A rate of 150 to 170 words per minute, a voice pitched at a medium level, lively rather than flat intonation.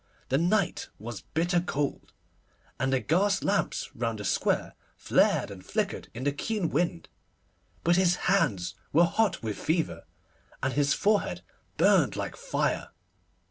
No: average, 140 wpm; medium, 165 Hz; wide, 6.0 semitones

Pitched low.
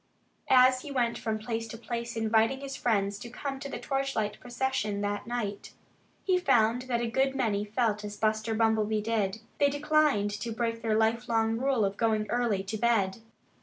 No: high, 230 Hz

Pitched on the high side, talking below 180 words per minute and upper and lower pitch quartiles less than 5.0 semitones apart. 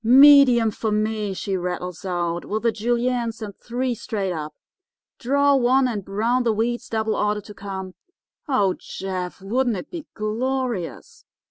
Yes: high, 220 Hz; average, 150 wpm; average, 4.0 semitones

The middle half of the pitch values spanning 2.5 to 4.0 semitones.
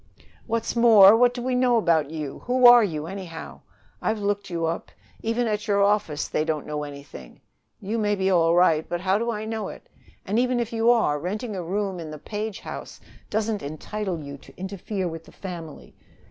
No: average, 5.3 semitones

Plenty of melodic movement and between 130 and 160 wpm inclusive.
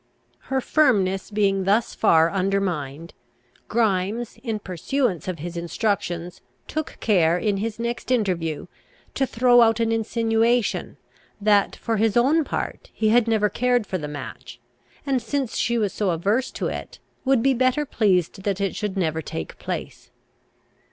No: average, 4.4 semitones; average, 150 wpm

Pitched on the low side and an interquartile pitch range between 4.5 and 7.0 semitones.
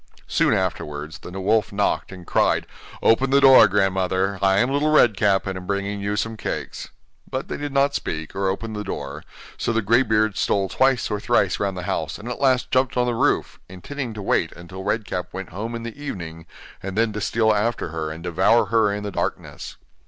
No: low, 105 Hz; average, 3.7 semitones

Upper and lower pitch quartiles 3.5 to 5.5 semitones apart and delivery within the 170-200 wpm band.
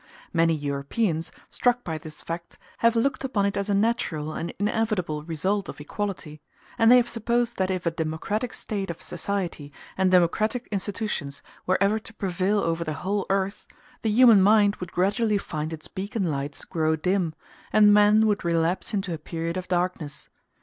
Yes: average, 4.4 semitones; average, 175 wpm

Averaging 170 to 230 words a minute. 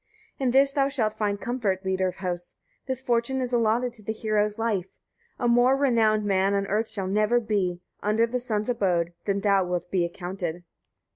Yes: average, 195 wpm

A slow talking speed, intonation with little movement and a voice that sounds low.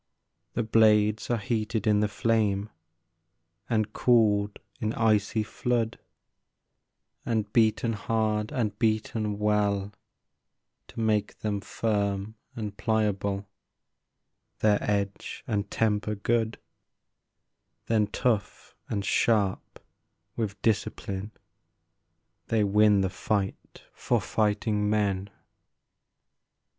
Yes: slow, 95 wpm; narrow, 1.4 semitones; low, 105 Hz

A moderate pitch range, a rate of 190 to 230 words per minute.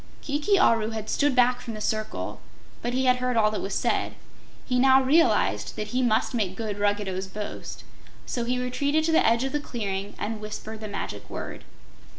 Yes: average, 3.5 semitones; average, 195 wpm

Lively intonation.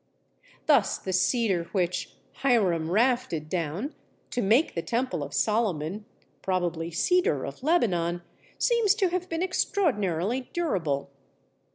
Yes: wide, 8.2 semitones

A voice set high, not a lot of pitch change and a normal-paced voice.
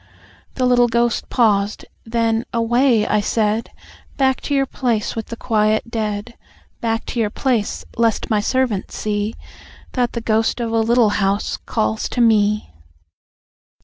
Yes: high, 225 Hz; narrow, 2.1 semitones; average, 145 wpm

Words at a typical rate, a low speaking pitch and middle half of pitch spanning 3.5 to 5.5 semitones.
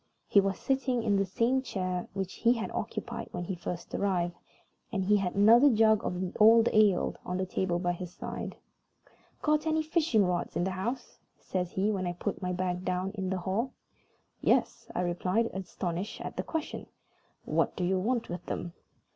No: average, 190 wpm; high, 190 Hz; average, 3.9 semitones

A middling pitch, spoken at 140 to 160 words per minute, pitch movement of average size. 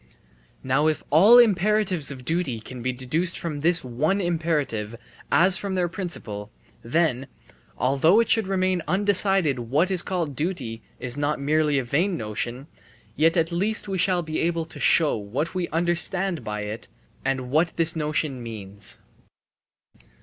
No: medium, 160 Hz; average, 155 wpm; wide, 5.7 semitones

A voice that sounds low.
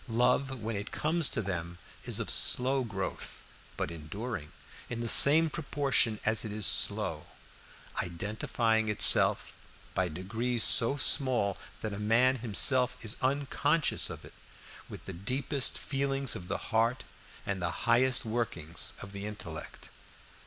Yes: low, 115 Hz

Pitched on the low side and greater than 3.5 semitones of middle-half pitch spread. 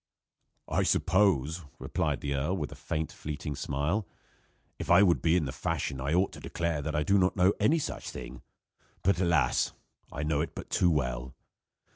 Yes: very low, 80 Hz; average, 4.2 semitones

